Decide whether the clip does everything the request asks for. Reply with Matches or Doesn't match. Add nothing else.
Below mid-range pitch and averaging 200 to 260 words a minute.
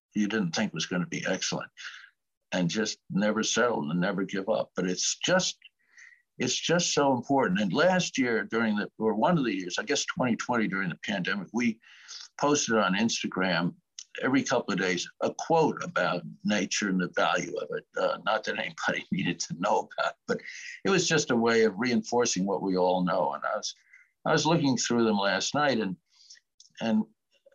Doesn't match